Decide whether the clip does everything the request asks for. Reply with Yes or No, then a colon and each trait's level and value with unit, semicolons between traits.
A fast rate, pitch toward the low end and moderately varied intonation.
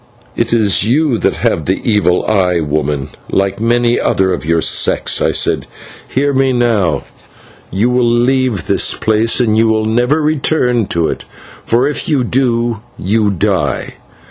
No: average, 160 wpm; low, 115 Hz; average, 4.1 semitones